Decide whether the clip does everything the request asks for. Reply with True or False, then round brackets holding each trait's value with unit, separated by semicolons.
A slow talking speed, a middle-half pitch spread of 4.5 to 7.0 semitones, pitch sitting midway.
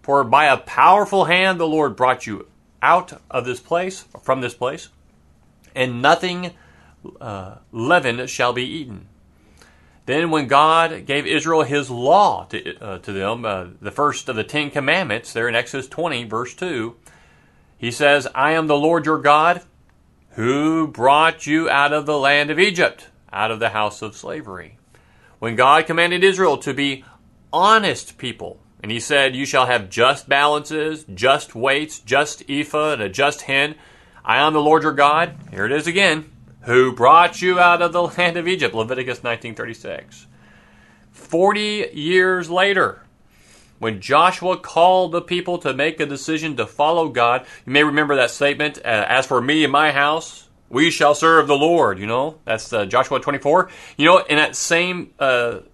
False (170 wpm; 4.8 semitones; 145 Hz)